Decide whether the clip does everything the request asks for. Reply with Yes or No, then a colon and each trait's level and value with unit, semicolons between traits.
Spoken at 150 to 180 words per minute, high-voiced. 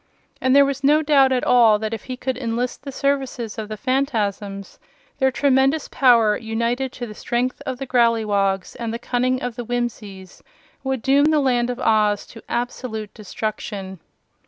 Yes: average, 175 wpm; high, 245 Hz